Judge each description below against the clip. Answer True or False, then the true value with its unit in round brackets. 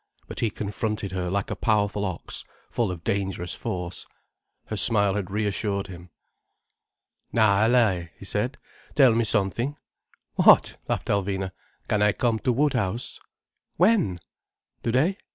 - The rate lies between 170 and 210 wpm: False (135 wpm)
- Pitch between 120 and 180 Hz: False (105 Hz)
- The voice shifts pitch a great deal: False (3.4 semitones)